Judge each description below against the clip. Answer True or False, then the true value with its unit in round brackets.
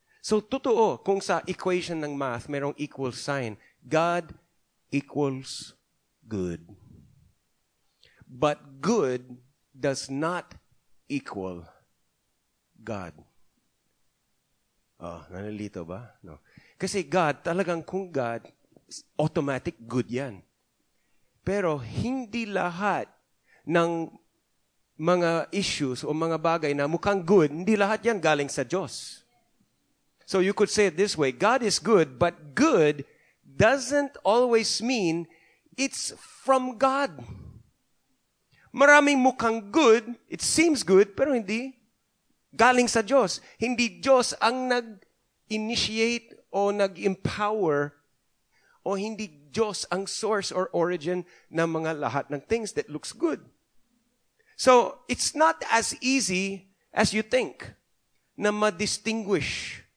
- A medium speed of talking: False (110 wpm)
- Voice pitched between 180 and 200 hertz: True (185 Hz)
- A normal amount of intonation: False (7.7 semitones)